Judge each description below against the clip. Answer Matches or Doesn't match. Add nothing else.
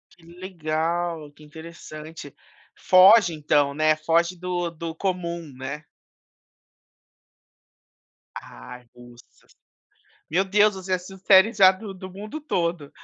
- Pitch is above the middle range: Doesn't match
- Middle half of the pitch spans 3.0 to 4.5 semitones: Matches